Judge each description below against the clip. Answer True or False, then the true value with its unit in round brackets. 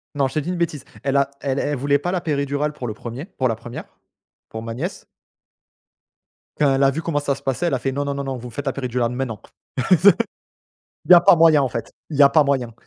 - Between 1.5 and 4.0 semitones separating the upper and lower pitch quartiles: True (2.8 semitones)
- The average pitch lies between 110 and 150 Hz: True (140 Hz)